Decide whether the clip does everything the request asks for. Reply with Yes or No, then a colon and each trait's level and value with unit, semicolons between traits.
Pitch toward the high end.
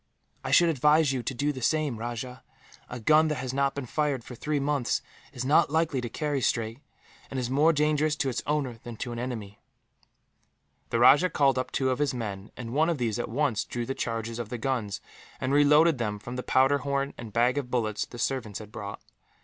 No: low, 130 Hz